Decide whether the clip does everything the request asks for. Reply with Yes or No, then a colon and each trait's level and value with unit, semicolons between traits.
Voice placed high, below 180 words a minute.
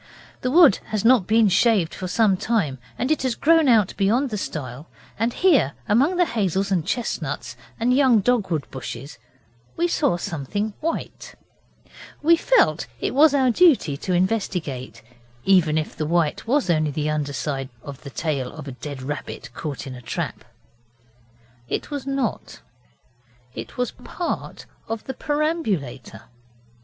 Yes: high, 195 Hz; average, 155 wpm